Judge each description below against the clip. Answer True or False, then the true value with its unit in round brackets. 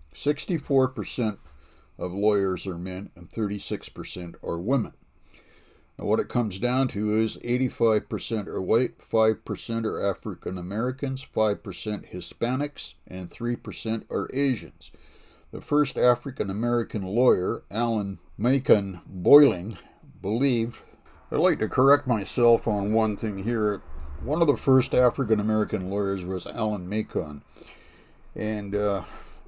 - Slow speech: True (130 wpm)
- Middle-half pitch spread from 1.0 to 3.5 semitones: False (4.0 semitones)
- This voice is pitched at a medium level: False (110 Hz)